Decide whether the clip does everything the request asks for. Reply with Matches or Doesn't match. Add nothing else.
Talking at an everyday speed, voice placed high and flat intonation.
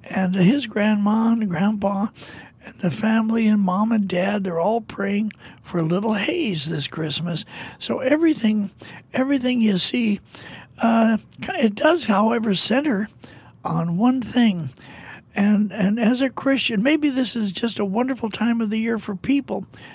Doesn't match